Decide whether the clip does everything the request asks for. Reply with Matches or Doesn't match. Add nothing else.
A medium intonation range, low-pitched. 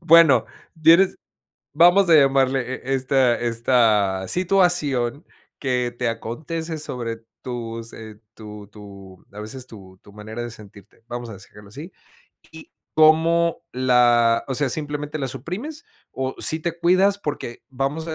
Doesn't match